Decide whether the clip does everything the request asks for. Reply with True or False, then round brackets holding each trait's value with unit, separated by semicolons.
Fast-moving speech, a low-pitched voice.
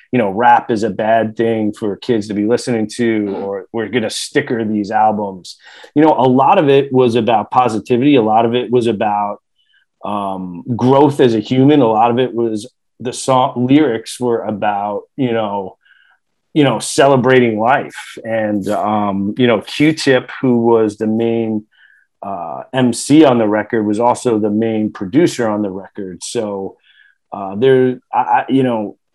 False (175 wpm; 115 Hz)